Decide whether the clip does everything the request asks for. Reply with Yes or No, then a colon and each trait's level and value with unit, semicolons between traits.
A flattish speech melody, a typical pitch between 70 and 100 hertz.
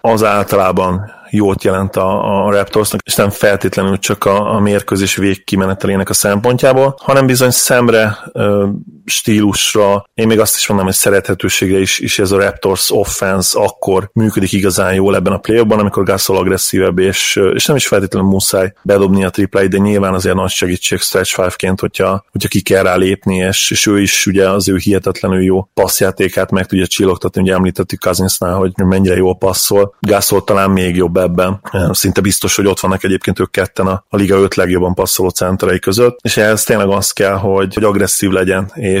Yes: narrow, 1.4 semitones; very low, 95 Hz